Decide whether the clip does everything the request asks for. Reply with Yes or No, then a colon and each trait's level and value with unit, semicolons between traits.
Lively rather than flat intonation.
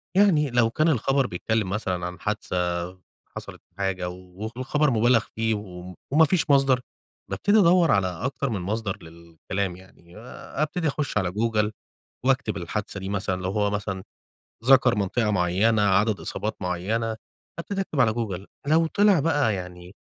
Yes: wide, 6.3 semitones